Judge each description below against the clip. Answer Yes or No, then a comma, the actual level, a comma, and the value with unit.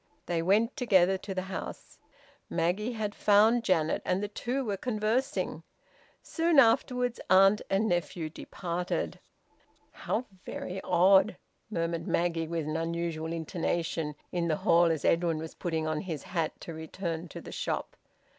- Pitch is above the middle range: No, medium, 175 Hz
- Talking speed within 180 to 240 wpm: No, average, 145 wpm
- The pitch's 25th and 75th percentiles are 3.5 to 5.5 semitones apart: Yes, average, 4.1 semitones